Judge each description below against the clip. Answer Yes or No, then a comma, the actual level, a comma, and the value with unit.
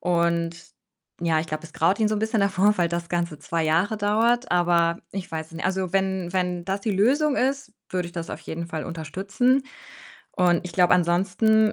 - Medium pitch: Yes, medium, 180 Hz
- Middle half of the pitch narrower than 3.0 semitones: No, average, 3.5 semitones